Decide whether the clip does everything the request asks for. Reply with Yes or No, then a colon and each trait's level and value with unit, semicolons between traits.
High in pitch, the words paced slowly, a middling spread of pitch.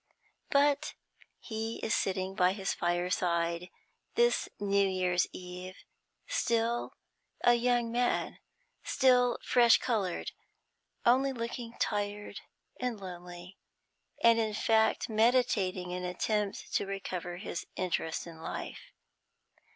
Yes: high, 205 Hz; slow, 105 wpm; average, 4.6 semitones